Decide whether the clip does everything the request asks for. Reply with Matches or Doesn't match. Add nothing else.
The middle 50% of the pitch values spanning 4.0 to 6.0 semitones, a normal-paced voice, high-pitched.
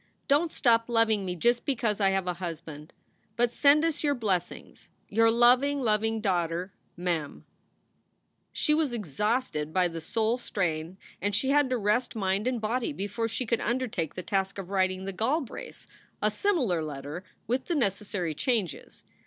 Matches